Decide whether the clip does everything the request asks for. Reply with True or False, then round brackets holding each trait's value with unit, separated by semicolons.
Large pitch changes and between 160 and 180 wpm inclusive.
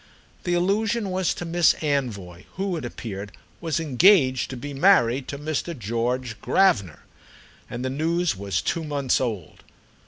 False (6.8 semitones; 150 wpm)